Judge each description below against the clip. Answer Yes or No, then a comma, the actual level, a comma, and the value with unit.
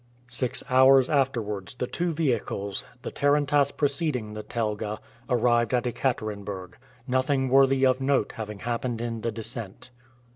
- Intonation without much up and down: No, average, 3.8 semitones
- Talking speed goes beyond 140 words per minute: No, slow, 135 wpm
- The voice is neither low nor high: No, low, 125 Hz